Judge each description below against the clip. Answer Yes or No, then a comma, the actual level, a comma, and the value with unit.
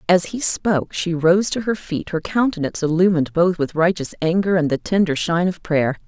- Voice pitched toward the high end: No, medium, 170 Hz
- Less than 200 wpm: No, fast, 205 wpm